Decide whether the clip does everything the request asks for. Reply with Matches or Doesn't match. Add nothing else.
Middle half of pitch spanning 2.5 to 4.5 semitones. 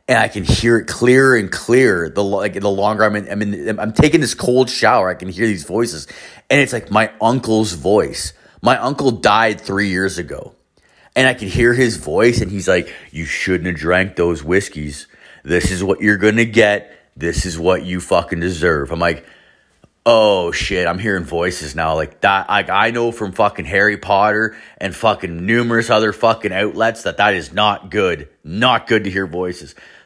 Matches